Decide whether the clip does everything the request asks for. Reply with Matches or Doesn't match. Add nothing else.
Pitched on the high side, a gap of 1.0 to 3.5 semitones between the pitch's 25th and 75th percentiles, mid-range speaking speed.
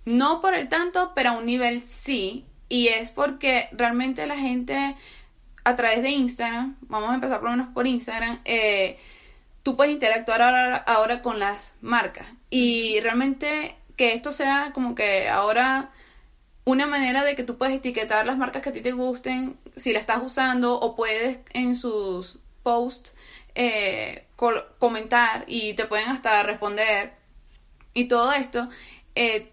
Matches